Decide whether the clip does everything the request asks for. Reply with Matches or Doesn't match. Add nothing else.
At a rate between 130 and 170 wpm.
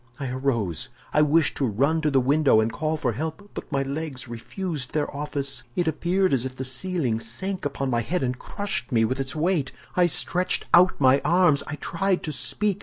Doesn't match